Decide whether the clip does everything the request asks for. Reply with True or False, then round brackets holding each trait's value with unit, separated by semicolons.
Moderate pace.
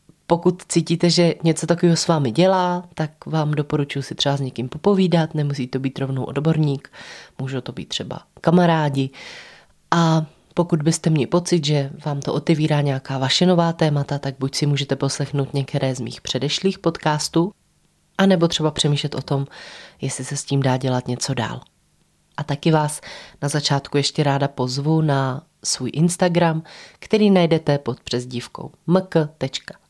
True (155 wpm)